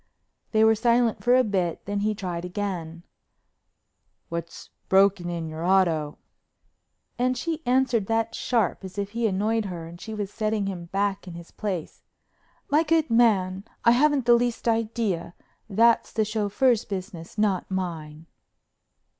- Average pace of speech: Yes, average, 150 wpm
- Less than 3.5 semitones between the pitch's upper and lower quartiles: No, average, 4.3 semitones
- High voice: Yes, high, 205 Hz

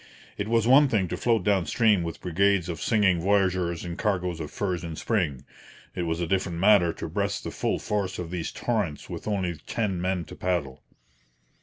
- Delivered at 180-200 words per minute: Yes, average, 195 wpm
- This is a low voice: Yes, very low, 90 Hz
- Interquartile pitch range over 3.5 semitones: No, average, 3.2 semitones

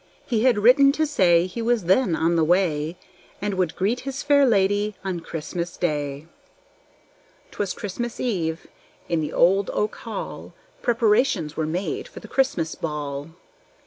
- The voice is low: No, high, 190 Hz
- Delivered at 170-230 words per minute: No, average, 150 wpm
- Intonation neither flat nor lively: No, wide, 6.1 semitones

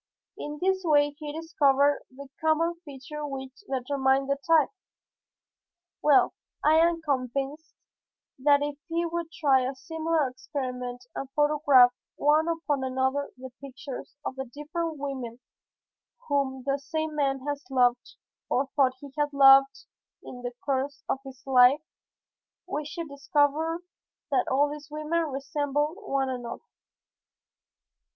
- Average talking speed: No, slow, 130 wpm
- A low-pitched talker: No, very high, 285 Hz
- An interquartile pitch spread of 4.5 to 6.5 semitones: No, narrow, 2.4 semitones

